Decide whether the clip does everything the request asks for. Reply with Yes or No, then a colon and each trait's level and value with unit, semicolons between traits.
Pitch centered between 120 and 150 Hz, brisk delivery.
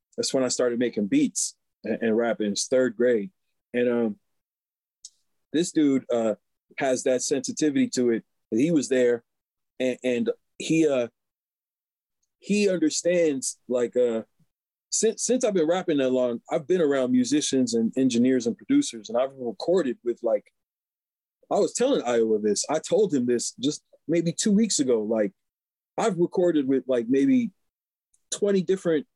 No: low, 135 Hz; average, 155 wpm